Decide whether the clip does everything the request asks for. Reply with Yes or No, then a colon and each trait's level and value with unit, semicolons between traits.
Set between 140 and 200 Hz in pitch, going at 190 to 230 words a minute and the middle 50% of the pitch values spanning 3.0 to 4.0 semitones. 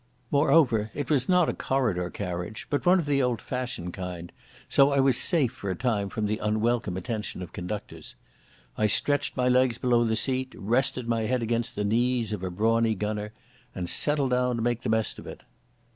No: low, 115 Hz; average, 200 wpm; average, 3.5 semitones